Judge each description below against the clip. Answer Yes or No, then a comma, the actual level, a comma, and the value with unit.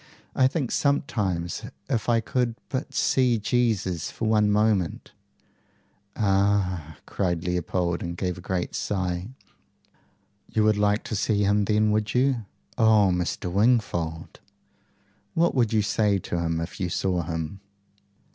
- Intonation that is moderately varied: Yes, average, 3.9 semitones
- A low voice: Yes, low, 100 Hz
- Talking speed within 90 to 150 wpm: Yes, average, 140 wpm